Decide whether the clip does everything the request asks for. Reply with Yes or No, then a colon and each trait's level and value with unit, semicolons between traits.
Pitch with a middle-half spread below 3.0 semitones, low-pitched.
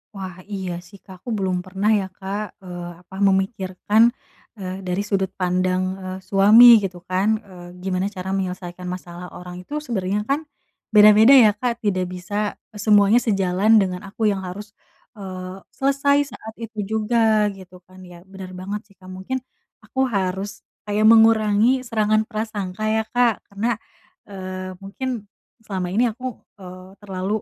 No: narrow, 2.5 semitones; high, 195 Hz